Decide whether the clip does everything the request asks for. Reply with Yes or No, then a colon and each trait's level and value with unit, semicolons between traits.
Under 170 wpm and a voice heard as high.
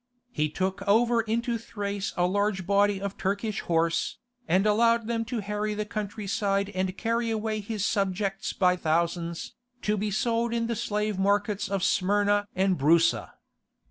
Yes: average, 160 wpm; high, 205 Hz